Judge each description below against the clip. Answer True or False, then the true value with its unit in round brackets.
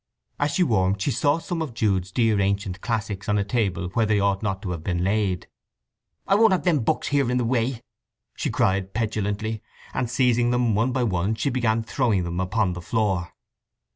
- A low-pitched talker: True (110 Hz)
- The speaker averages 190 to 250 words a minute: True (200 wpm)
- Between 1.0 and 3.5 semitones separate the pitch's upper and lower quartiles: False (4.1 semitones)